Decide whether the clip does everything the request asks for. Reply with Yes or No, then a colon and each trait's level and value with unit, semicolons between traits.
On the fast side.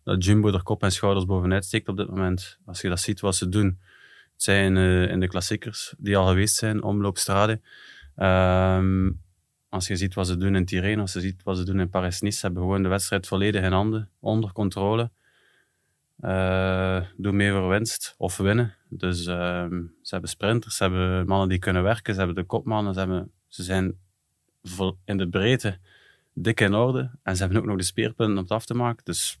Yes: fast, 205 wpm